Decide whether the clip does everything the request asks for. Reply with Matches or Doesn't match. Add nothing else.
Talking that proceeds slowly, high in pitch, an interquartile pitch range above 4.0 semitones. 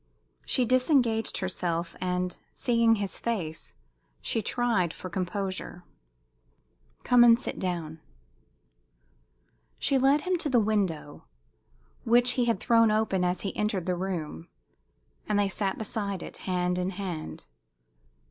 Matches